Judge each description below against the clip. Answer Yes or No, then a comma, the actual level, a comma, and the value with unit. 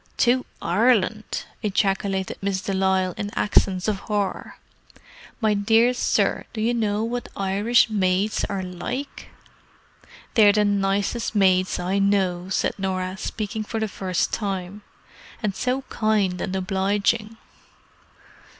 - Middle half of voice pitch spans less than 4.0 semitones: Yes, narrow, 2.4 semitones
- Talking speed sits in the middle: No, slow, 125 wpm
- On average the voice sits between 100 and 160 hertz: No, high, 200 Hz